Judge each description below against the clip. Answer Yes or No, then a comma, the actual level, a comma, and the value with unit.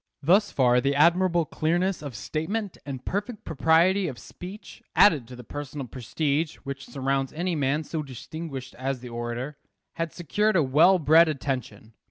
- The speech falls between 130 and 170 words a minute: Yes, average, 160 wpm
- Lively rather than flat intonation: No, average, 4.6 semitones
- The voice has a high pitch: No, medium, 150 Hz